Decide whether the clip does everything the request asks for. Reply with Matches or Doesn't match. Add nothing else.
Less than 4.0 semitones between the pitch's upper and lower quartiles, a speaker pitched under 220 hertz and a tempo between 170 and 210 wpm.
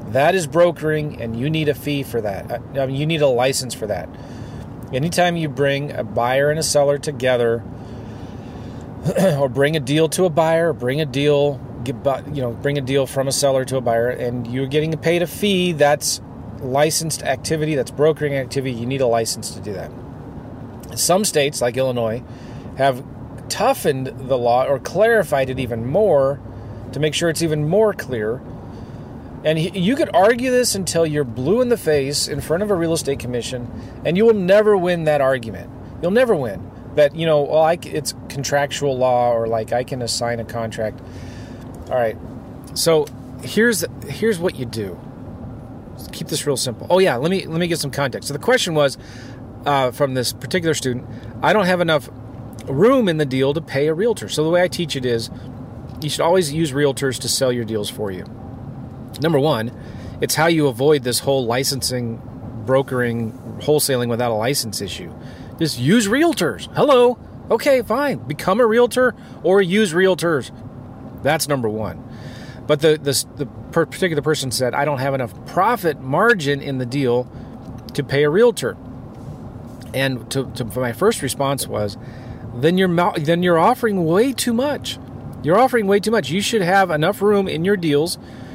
Doesn't match